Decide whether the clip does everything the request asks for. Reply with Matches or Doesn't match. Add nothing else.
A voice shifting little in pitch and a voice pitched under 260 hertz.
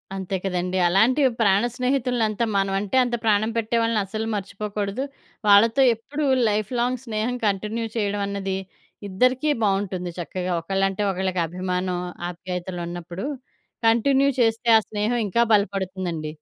Doesn't match